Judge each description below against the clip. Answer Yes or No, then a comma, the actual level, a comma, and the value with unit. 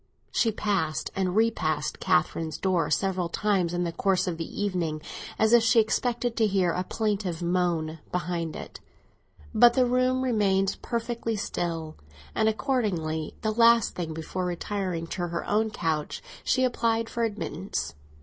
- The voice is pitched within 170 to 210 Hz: Yes, high, 190 Hz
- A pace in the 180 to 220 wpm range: No, average, 150 wpm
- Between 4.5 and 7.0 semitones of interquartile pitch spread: Yes, average, 4.9 semitones